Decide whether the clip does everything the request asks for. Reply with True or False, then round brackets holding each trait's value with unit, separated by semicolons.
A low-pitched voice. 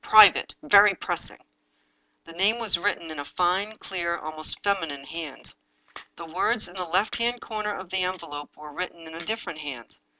False (175 Hz)